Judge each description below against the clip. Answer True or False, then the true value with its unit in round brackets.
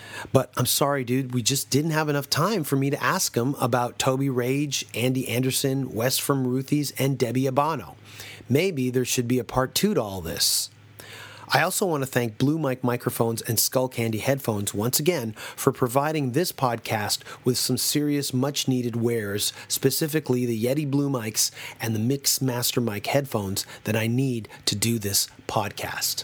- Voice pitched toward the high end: False (130 Hz)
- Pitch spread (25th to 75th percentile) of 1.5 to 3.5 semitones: True (2.9 semitones)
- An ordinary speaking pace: True (180 wpm)